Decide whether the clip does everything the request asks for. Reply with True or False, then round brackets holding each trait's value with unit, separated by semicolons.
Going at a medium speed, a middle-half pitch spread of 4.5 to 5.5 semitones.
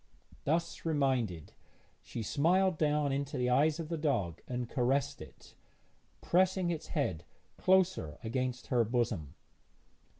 False (125 wpm; 5.1 semitones)